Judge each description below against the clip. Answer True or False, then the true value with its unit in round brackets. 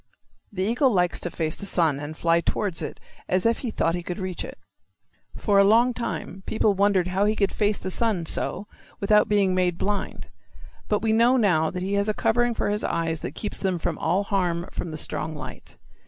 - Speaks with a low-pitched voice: False (195 Hz)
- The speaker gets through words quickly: True (215 wpm)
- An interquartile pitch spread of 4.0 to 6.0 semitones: False (3.4 semitones)